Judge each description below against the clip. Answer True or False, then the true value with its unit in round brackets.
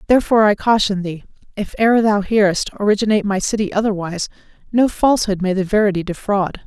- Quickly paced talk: False (160 wpm)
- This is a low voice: False (205 Hz)